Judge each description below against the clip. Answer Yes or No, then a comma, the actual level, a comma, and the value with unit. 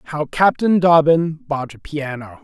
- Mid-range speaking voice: Yes, medium, 150 Hz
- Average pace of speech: Yes, average, 150 wpm